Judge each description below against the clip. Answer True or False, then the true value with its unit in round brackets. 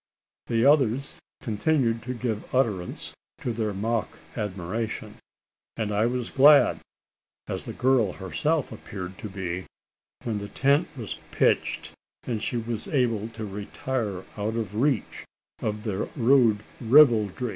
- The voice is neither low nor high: False (115 Hz)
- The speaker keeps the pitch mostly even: False (3.5 semitones)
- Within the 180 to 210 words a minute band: False (135 wpm)